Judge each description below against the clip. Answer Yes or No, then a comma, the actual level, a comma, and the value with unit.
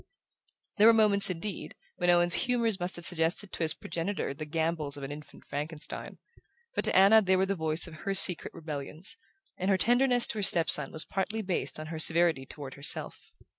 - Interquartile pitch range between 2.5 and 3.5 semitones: No, average, 4.0 semitones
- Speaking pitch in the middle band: Yes, medium, 175 Hz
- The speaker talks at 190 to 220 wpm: Yes, average, 200 wpm